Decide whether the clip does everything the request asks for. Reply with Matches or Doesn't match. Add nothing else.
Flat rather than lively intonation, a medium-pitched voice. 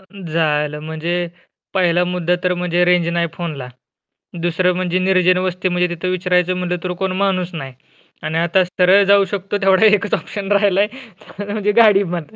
Matches